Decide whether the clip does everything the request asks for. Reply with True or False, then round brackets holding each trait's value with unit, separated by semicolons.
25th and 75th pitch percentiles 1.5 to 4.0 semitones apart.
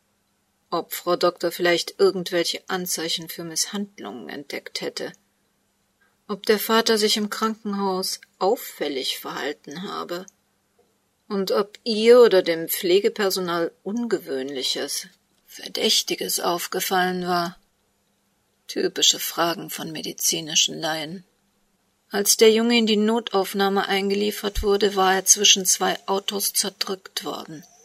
True (3.4 semitones)